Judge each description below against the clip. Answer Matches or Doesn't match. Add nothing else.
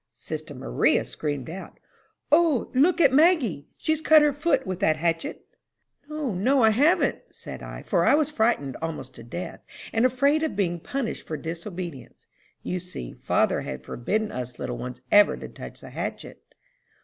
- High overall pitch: Matches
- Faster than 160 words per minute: Matches